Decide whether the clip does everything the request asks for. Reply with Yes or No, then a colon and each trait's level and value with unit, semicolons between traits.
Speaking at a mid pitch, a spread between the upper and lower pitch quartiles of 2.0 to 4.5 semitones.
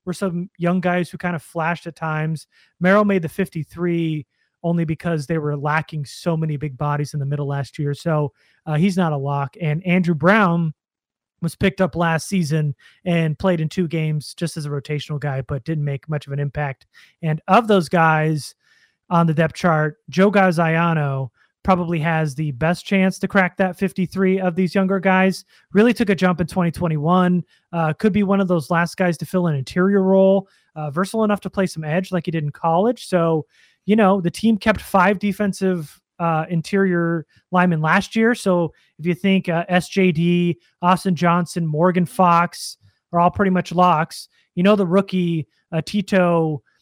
Yes: medium, 170 Hz; average, 3.2 semitones